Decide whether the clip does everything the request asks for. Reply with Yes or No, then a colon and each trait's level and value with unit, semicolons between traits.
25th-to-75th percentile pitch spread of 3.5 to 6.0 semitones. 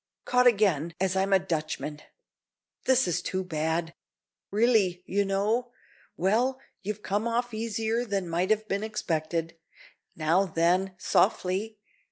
Yes: average, 4.1 semitones